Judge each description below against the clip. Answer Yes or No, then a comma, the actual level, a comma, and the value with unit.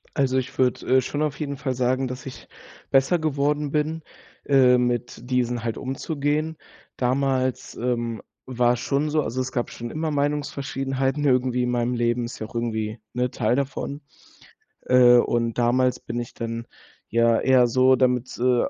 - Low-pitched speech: Yes, low, 130 Hz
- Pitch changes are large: No, narrow, 2.4 semitones